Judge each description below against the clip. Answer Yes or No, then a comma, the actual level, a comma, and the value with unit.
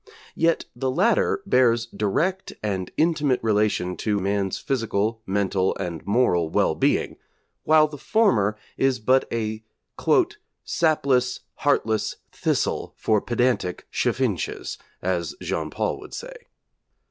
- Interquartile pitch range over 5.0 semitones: Yes, wide, 5.5 semitones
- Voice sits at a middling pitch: No, low, 115 Hz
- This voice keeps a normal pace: No, slow, 115 wpm